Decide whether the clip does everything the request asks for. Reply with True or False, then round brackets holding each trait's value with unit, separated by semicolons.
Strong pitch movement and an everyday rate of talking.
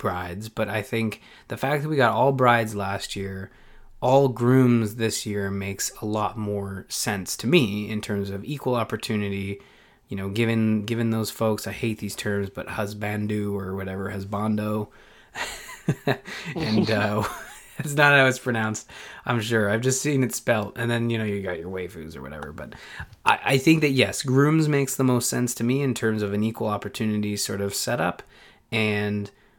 False (3.2 semitones; 185 wpm)